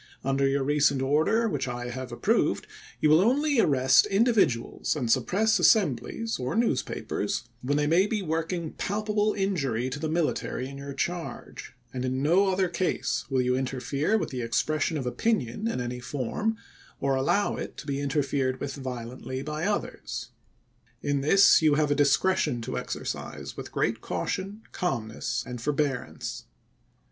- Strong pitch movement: Yes, wide, 6.4 semitones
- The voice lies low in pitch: No, medium, 145 Hz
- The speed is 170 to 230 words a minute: No, average, 160 wpm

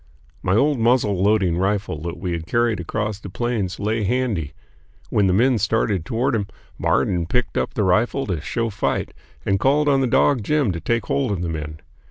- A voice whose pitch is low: Yes, low, 105 Hz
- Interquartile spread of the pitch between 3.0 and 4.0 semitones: No, average, 4.8 semitones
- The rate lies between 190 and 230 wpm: Yes, average, 200 wpm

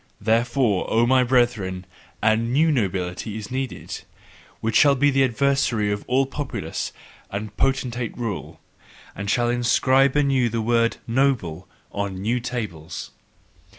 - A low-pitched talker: Yes, low, 120 Hz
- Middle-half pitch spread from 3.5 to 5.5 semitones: Yes, average, 4.2 semitones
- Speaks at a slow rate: Yes, slow, 130 wpm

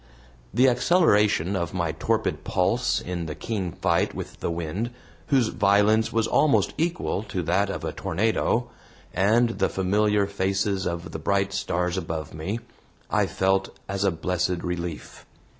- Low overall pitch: Yes, very low, 95 Hz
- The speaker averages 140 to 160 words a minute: Yes, average, 150 wpm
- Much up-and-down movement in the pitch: No, average, 3.4 semitones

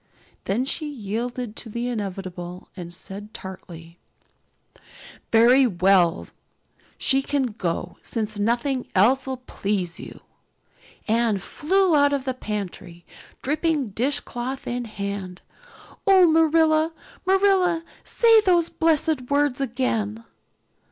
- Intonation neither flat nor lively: No, wide, 6.6 semitones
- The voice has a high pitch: Yes, high, 245 Hz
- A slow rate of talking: Yes, slow, 110 wpm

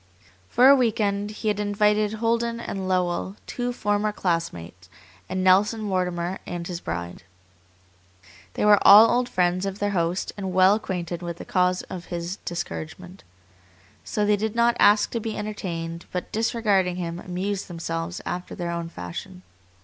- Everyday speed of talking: Yes, average, 160 wpm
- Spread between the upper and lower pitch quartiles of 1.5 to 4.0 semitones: Yes, average, 3.3 semitones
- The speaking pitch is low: No, high, 190 Hz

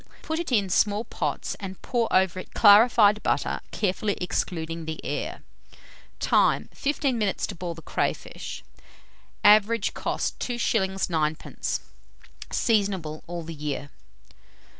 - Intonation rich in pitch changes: No, average, 4.8 semitones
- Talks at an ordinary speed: No, slow, 120 wpm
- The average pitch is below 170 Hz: No, high, 195 Hz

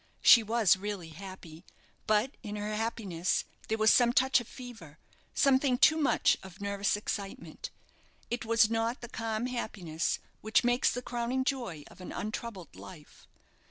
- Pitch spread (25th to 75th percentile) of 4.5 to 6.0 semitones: No, average, 3.8 semitones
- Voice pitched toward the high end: Yes, high, 220 Hz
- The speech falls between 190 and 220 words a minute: No, average, 155 wpm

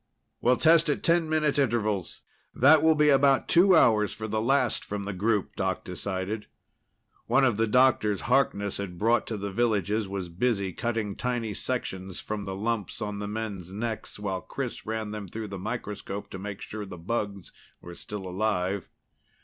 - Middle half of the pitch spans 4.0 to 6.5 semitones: No, average, 3.4 semitones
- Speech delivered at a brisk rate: No, average, 175 wpm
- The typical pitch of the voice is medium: No, low, 105 Hz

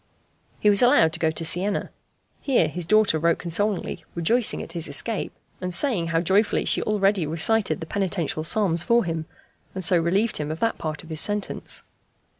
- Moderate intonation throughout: Yes, average, 4.3 semitones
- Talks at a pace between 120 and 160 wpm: No, average, 185 wpm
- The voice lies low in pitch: No, medium, 175 Hz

